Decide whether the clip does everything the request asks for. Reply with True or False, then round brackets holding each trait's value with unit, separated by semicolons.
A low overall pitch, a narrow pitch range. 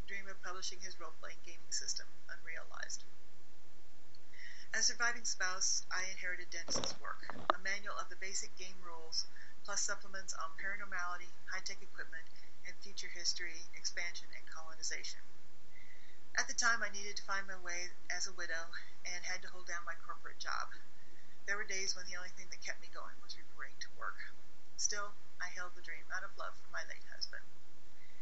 False (185 Hz; 2.1 semitones)